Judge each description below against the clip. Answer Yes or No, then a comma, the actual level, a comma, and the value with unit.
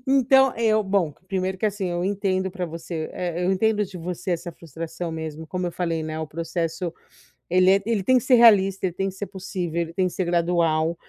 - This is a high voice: No, medium, 180 Hz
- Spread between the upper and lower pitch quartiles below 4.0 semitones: Yes, average, 2.7 semitones